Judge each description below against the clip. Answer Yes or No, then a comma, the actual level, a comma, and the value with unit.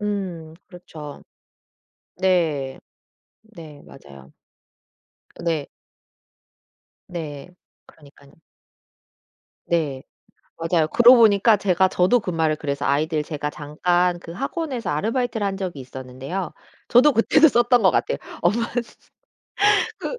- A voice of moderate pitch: Yes, medium, 175 Hz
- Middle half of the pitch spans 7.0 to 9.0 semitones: No, wide, 5.8 semitones